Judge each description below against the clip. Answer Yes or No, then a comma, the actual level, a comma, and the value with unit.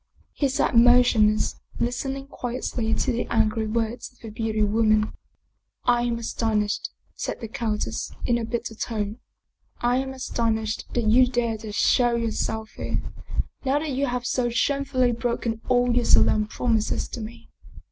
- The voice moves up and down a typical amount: No, narrow, 2.0 semitones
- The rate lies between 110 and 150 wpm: No, average, 165 wpm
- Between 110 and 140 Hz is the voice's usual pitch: No, high, 235 Hz